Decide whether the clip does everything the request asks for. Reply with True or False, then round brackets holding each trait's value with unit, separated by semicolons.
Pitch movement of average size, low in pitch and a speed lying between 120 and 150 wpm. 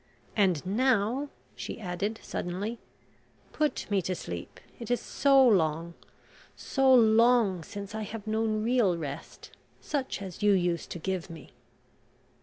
False (4.9 semitones; 205 Hz; 140 wpm)